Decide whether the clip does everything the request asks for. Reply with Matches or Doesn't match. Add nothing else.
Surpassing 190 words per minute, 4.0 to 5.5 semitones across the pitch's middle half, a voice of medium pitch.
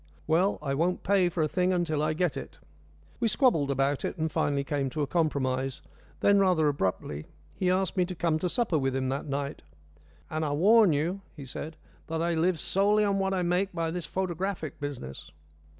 Matches